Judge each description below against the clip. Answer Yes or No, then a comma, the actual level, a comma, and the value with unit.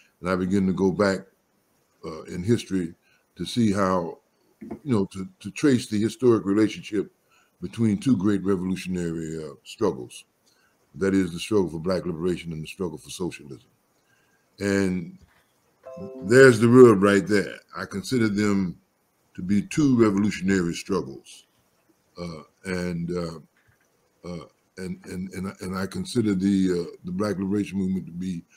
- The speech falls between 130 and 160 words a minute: Yes, average, 145 wpm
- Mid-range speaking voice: No, very low, 95 Hz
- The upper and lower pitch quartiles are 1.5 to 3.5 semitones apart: Yes, narrow, 2.5 semitones